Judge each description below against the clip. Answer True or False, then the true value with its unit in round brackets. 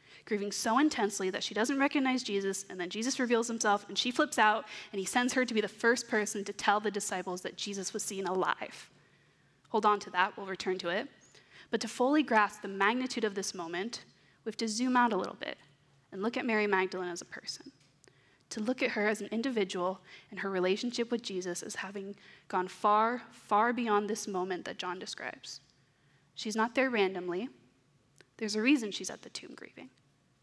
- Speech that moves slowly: False (205 wpm)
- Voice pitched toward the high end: True (205 Hz)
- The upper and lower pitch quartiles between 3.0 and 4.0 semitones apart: True (3.5 semitones)